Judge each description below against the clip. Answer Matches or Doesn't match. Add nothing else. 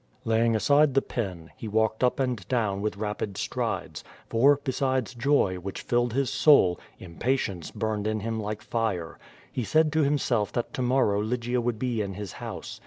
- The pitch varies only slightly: Doesn't match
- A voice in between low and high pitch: Doesn't match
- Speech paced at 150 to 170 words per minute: Doesn't match